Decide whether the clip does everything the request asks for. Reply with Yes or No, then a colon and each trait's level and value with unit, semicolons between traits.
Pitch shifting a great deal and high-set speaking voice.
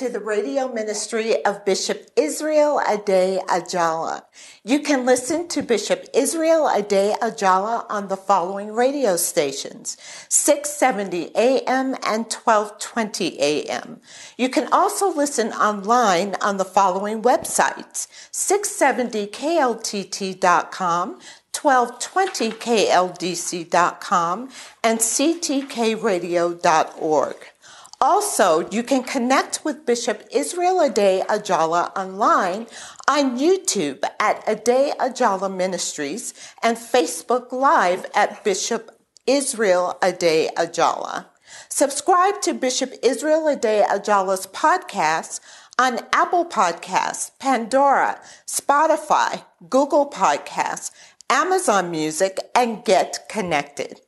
Yes: wide, 6.4 semitones; high, 230 Hz